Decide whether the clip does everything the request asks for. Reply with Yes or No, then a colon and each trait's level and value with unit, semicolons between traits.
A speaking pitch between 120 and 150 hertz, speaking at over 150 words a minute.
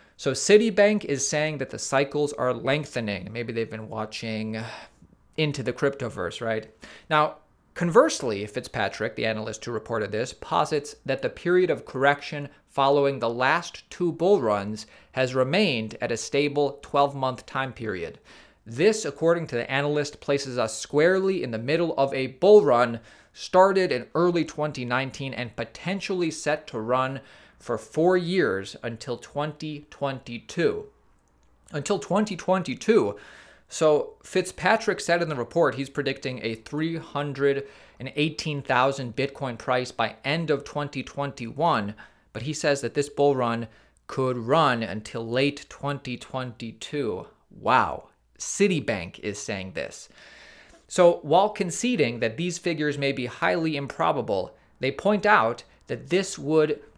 No: medium, 140 Hz; slow, 135 wpm